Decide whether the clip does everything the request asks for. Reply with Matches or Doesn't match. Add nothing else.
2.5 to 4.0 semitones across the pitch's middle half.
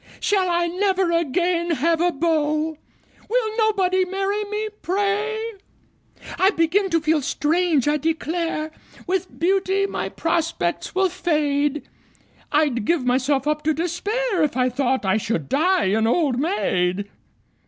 Doesn't match